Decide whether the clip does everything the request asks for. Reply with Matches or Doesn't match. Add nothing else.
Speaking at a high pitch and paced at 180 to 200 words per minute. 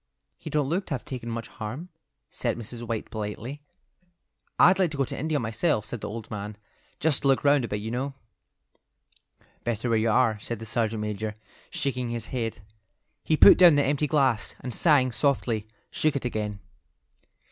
Doesn't match